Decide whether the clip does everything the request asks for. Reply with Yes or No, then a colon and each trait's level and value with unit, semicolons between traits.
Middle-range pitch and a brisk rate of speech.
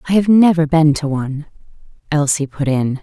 No: medium, 155 Hz; average, 180 wpm